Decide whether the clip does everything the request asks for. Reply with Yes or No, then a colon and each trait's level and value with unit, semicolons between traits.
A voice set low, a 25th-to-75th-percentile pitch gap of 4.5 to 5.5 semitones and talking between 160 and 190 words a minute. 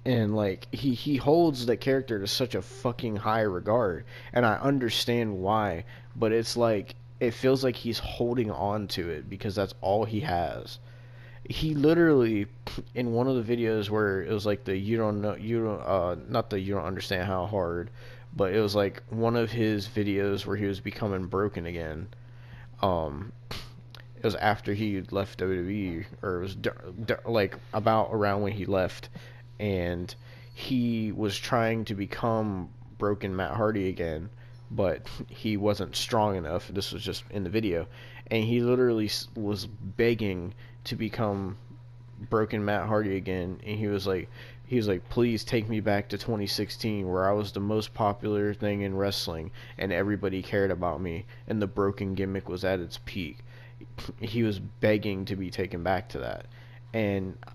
No: low, 110 Hz; average, 3.3 semitones; average, 175 wpm